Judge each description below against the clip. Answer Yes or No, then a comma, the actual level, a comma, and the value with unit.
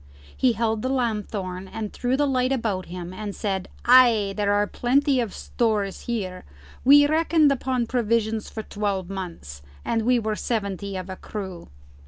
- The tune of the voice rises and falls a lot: No, average, 4.1 semitones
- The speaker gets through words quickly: No, average, 165 wpm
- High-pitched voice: Yes, high, 220 Hz